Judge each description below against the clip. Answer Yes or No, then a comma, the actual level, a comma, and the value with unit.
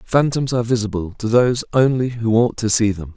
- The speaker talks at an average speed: No, fast, 210 wpm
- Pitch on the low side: Yes, low, 115 Hz